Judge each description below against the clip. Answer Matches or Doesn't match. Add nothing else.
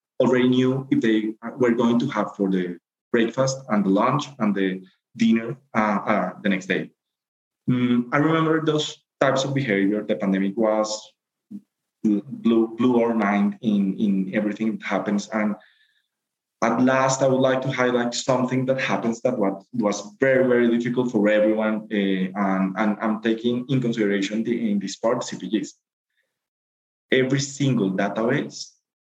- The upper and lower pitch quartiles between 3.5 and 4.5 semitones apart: Matches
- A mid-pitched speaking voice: Doesn't match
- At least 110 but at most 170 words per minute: Matches